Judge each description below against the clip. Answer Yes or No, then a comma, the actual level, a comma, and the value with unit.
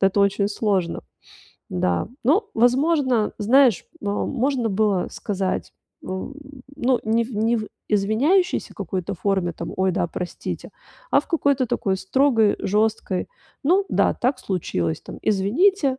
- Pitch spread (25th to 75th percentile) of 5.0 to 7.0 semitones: Yes, wide, 5.5 semitones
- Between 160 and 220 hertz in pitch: Yes, high, 215 Hz